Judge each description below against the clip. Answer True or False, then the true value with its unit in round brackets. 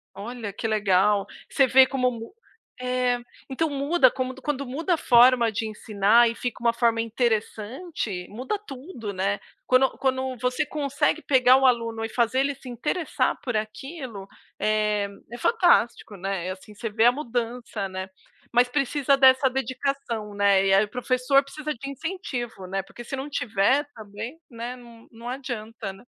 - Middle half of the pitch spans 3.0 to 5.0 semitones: True (3.7 semitones)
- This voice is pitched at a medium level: False (245 Hz)